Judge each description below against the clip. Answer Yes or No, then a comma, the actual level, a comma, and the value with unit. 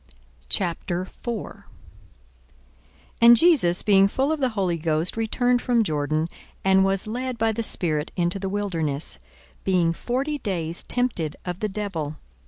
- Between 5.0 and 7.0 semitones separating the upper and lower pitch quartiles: Yes, wide, 5.6 semitones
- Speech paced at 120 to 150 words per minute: Yes, average, 140 wpm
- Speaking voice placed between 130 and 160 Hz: No, high, 195 Hz